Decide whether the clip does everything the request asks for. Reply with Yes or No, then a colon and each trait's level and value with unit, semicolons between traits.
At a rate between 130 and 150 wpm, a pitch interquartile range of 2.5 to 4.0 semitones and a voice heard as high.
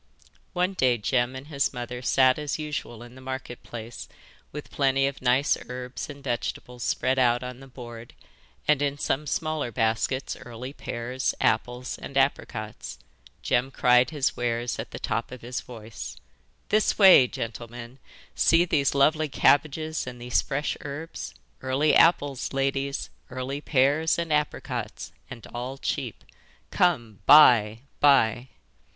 No: average, 145 wpm; average, 2.9 semitones; low, 130 Hz